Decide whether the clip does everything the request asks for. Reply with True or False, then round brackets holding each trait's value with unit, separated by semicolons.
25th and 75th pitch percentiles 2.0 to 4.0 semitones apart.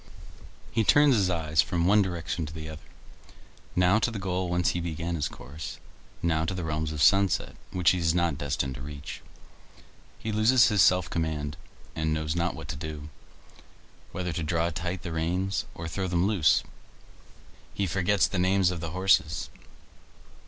True (3.0 semitones)